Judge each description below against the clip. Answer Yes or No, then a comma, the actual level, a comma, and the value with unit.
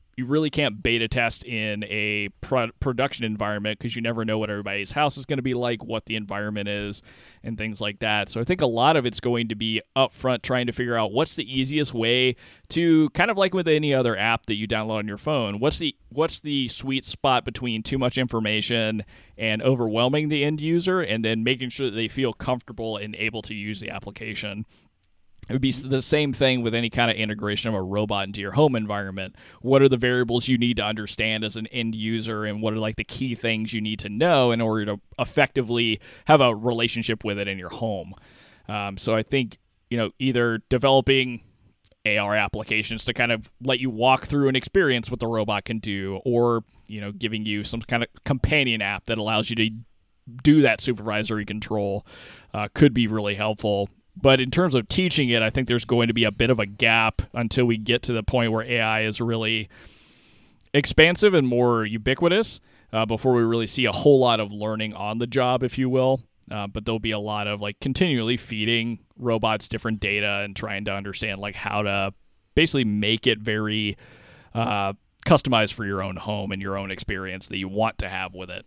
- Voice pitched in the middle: No, low, 115 Hz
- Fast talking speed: Yes, fast, 215 wpm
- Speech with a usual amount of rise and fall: Yes, average, 3.2 semitones